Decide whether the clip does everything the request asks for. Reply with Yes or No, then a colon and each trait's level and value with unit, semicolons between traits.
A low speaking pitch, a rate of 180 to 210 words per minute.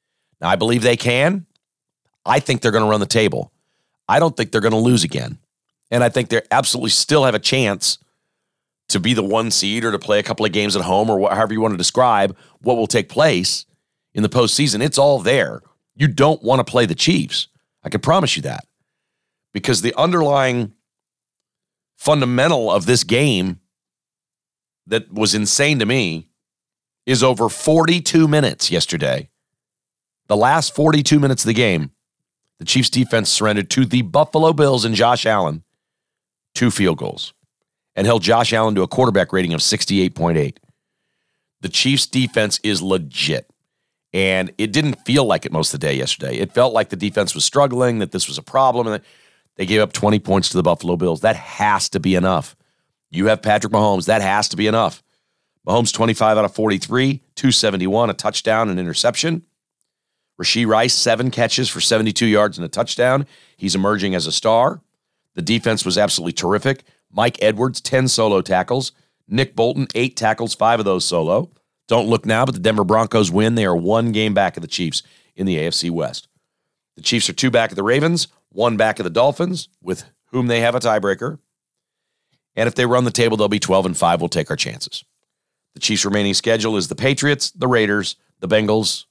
Yes: low, 115 Hz; average, 190 wpm